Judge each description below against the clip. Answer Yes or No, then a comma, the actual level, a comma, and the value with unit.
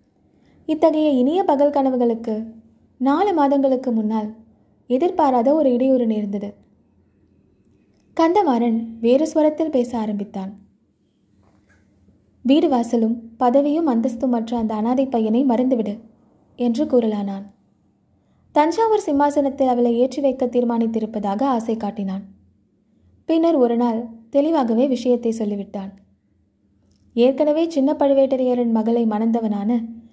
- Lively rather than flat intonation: No, average, 4.4 semitones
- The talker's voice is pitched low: No, high, 235 Hz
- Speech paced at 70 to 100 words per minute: Yes, average, 90 wpm